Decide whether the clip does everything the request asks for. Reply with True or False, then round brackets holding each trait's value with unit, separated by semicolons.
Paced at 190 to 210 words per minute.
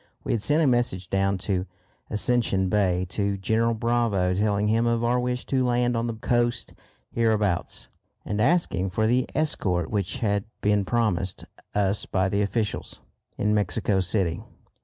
False (160 wpm)